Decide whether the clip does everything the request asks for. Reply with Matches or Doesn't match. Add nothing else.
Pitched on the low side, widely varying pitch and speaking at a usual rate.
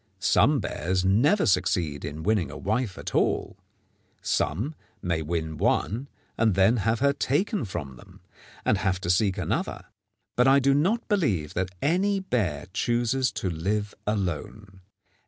Matches